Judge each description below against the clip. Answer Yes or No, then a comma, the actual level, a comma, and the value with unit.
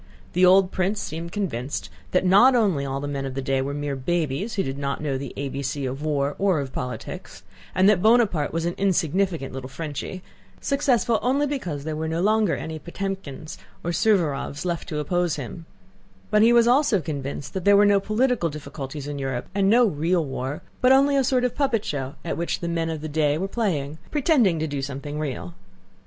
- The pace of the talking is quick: Yes, fast, 210 wpm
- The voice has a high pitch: No, medium, 165 Hz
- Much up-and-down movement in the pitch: Yes, wide, 6.1 semitones